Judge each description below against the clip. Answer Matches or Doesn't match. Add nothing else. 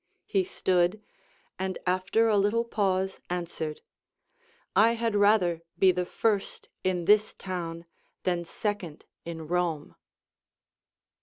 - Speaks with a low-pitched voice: Doesn't match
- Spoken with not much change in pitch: Doesn't match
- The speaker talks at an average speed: Doesn't match